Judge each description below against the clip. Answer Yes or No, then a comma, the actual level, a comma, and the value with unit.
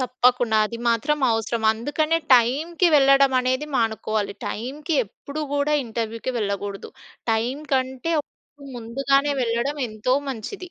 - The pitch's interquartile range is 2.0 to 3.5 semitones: No, average, 4.1 semitones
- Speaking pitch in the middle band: No, very high, 255 Hz